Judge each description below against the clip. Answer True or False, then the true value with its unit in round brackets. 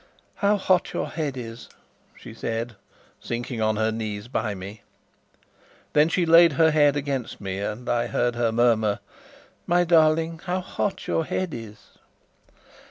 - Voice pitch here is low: True (120 Hz)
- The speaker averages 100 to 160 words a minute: True (150 wpm)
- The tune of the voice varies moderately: False (6.6 semitones)